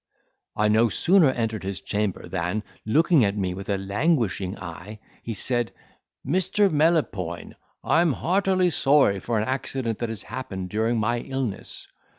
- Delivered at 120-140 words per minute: No, average, 150 wpm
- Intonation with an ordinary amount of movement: No, wide, 6.3 semitones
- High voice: No, low, 115 Hz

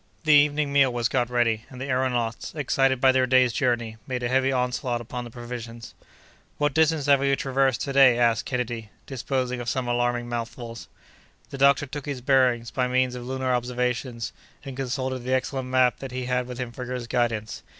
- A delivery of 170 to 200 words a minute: Yes, average, 195 wpm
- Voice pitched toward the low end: Yes, low, 125 Hz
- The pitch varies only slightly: Yes, narrow, 1.7 semitones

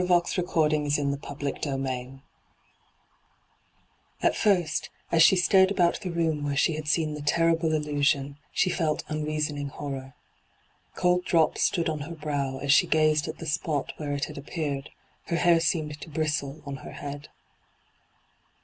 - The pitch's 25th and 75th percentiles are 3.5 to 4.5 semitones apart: No, narrow, 2.6 semitones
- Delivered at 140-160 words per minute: Yes, average, 150 wpm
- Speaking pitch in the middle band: Yes, medium, 150 Hz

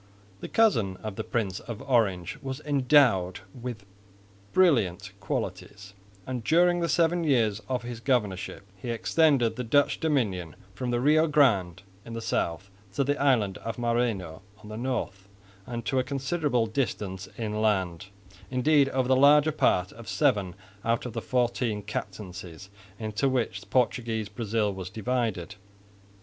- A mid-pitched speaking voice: No, low, 115 Hz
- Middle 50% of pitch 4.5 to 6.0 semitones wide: Yes, average, 4.9 semitones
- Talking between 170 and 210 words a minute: No, average, 145 wpm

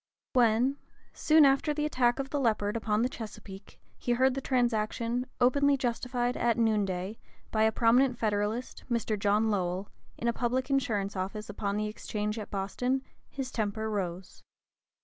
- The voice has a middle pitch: No, high, 230 Hz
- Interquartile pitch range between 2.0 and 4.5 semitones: Yes, average, 3.3 semitones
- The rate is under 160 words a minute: Yes, average, 150 wpm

